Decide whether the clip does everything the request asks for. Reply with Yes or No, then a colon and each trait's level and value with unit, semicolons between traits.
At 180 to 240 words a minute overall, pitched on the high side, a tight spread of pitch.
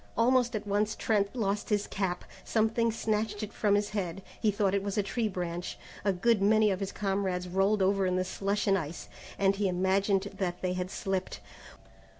Yes: average, 195 wpm; high, 200 Hz; narrow, 2.0 semitones